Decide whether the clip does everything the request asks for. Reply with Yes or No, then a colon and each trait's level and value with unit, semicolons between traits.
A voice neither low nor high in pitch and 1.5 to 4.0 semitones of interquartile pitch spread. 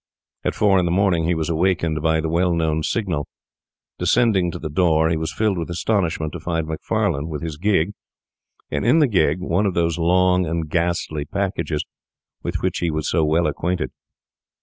No: very low, 85 Hz; narrow, 2.5 semitones